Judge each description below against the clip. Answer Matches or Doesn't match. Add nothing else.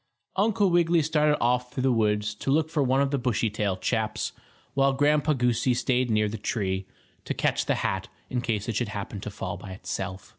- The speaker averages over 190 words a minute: Matches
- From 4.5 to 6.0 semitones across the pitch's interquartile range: Matches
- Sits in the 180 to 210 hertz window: Doesn't match